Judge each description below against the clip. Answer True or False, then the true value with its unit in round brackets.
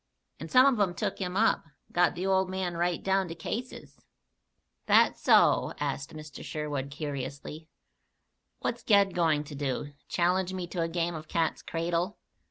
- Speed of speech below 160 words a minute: False (165 wpm)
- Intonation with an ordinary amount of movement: True (3.7 semitones)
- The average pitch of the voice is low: False (170 Hz)